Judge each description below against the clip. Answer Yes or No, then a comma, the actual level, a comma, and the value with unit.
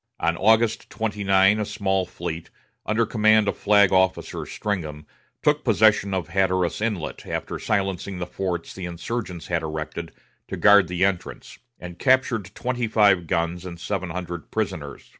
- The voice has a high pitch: No, very low, 95 Hz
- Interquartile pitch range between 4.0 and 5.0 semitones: No, average, 3.4 semitones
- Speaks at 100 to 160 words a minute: Yes, average, 150 wpm